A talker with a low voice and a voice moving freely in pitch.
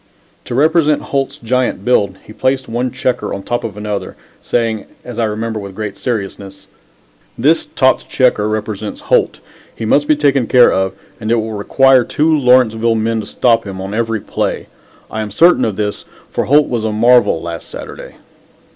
No: low, 115 Hz; average, 3.4 semitones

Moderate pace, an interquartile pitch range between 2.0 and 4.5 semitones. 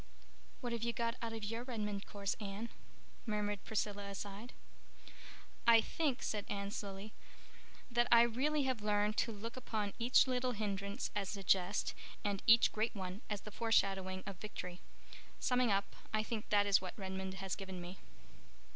Yes: average, 165 wpm; average, 2.8 semitones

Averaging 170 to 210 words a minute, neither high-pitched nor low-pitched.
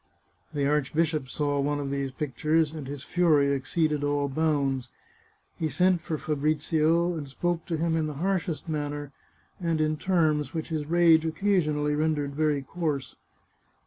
No: average, 150 wpm; medium, 155 Hz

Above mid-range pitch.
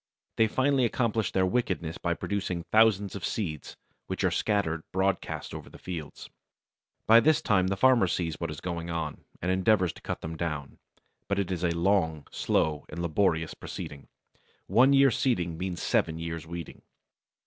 No: very low, 90 Hz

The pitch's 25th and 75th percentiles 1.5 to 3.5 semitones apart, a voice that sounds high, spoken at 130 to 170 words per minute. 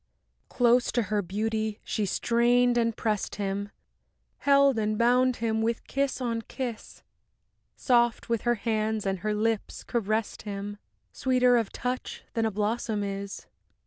Yes: narrow, 2.4 semitones; high, 225 Hz; average, 145 wpm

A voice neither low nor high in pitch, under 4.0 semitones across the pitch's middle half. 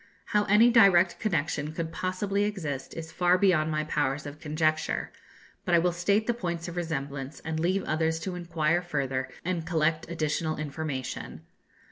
Yes: medium, 165 Hz; average, 3.0 semitones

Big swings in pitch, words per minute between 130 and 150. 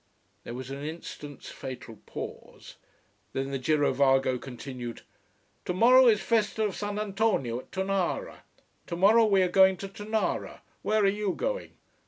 Yes: wide, 7.7 semitones; average, 140 wpm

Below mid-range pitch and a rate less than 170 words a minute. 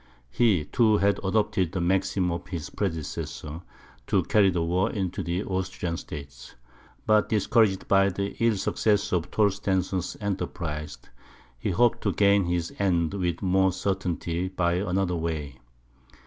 Yes: very low, 95 Hz; average, 140 wpm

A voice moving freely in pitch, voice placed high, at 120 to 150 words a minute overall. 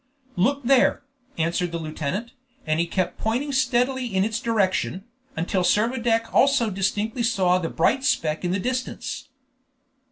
Yes: wide, 5.7 semitones; high, 215 Hz; average, 140 wpm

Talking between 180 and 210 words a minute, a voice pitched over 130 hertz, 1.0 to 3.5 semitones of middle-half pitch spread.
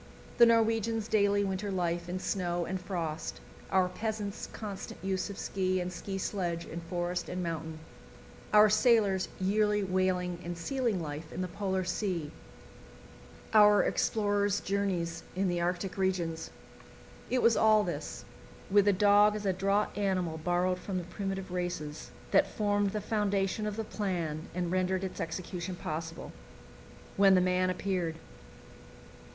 No: average, 145 wpm; high, 190 Hz; narrow, 2.6 semitones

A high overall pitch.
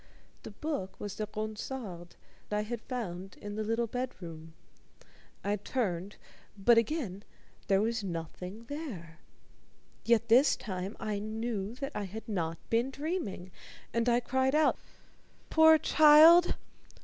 Yes: high, 220 Hz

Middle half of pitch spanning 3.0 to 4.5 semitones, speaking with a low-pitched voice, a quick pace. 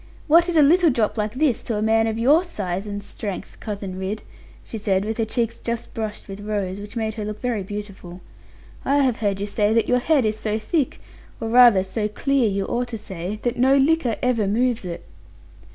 No: average, 3.4 semitones; high, 220 Hz; fast, 215 wpm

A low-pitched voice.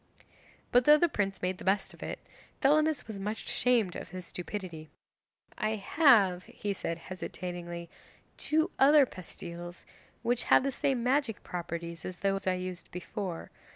No: high, 195 Hz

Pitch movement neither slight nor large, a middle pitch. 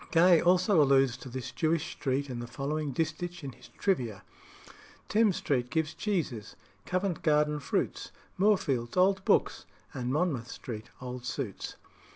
No: wide, 5.7 semitones; medium, 150 Hz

